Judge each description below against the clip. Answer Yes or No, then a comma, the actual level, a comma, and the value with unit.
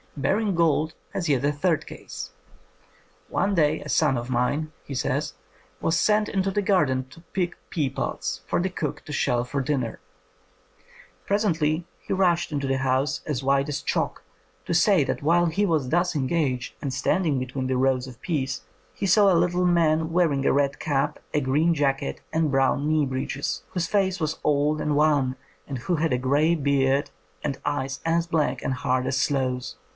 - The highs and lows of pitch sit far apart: No, average, 4.1 semitones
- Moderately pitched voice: Yes, medium, 150 Hz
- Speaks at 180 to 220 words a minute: Yes, average, 185 wpm